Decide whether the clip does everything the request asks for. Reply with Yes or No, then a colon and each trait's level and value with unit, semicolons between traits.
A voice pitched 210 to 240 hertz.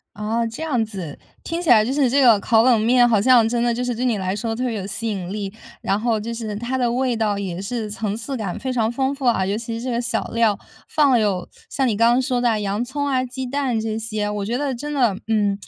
Yes: high, 230 Hz